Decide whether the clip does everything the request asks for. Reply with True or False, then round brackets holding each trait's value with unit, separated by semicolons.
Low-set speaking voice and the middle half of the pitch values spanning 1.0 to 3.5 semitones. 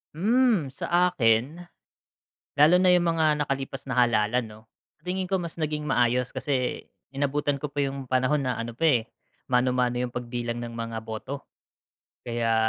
False (130 Hz; 4.0 semitones)